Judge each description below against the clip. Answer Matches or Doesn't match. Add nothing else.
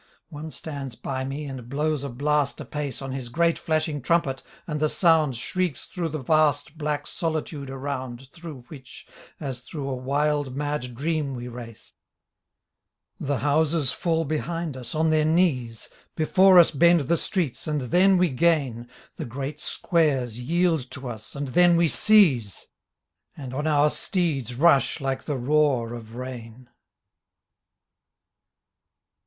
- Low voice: Doesn't match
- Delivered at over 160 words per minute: Doesn't match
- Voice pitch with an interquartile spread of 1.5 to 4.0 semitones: Matches